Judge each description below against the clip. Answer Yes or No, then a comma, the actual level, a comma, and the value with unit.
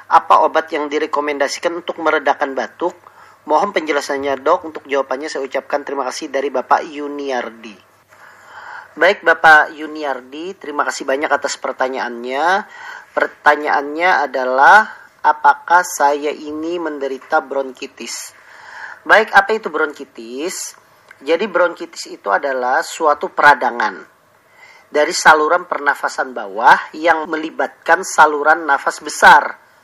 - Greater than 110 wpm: No, average, 105 wpm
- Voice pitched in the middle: Yes, medium, 150 Hz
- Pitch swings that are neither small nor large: Yes, average, 3.8 semitones